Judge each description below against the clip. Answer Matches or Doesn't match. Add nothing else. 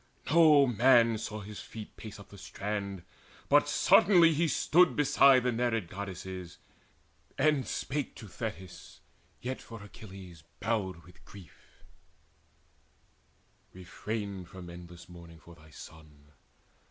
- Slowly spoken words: Matches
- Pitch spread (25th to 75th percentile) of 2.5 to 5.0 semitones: Doesn't match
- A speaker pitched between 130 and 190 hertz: Doesn't match